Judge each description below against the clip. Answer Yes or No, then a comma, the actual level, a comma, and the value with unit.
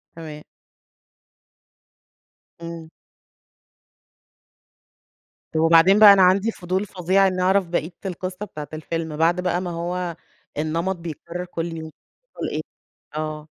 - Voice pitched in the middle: Yes, medium, 175 Hz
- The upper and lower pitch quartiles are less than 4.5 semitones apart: Yes, narrow, 2.4 semitones